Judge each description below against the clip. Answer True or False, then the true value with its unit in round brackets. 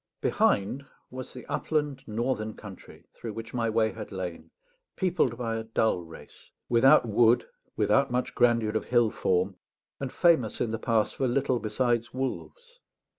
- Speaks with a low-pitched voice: True (115 Hz)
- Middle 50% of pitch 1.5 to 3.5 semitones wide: True (2.9 semitones)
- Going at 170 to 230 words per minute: False (155 wpm)